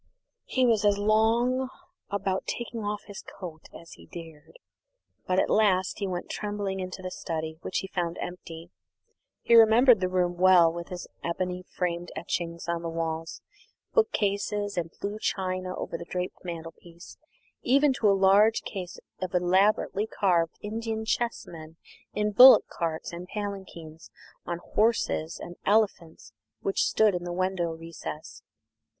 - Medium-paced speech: Yes, average, 145 wpm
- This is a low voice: No, medium, 185 Hz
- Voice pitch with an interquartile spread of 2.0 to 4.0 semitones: Yes, average, 3.5 semitones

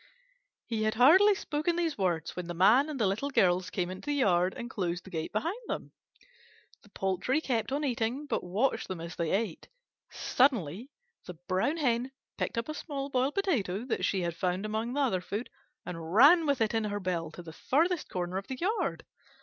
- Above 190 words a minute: Yes, fast, 205 wpm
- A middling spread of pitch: No, wide, 7.4 semitones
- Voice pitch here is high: Yes, high, 220 Hz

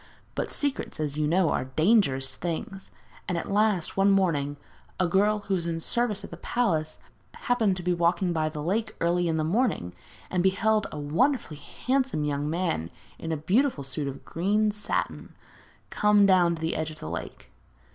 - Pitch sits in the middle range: Yes, medium, 175 Hz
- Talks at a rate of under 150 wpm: No, average, 185 wpm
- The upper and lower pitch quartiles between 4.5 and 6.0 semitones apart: Yes, average, 5.1 semitones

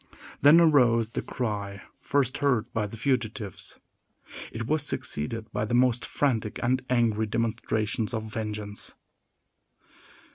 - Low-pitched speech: Yes, low, 115 Hz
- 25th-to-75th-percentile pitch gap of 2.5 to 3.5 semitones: Yes, average, 2.9 semitones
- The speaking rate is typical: No, slow, 120 wpm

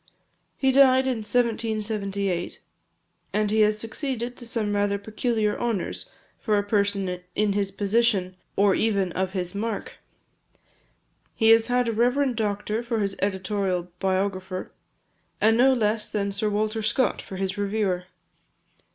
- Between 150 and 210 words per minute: No, average, 140 wpm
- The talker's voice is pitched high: Yes, high, 210 Hz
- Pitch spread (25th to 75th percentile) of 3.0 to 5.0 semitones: No, narrow, 2.5 semitones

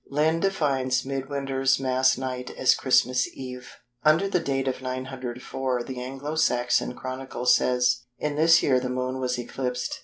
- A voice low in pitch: Yes, low, 130 Hz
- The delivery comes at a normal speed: Yes, average, 150 wpm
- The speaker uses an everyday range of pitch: No, narrow, 1.4 semitones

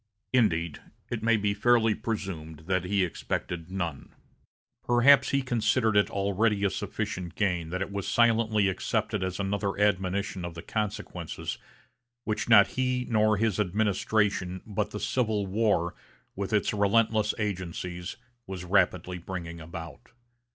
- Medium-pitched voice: No, low, 100 Hz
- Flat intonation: No, average, 3.2 semitones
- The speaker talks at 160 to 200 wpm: No, slow, 135 wpm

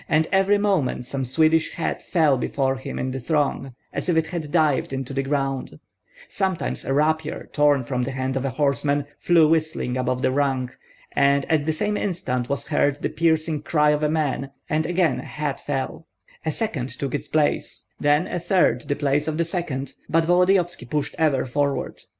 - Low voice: No, medium, 145 Hz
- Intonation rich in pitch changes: No, average, 3.1 semitones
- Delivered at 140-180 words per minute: No, average, 190 wpm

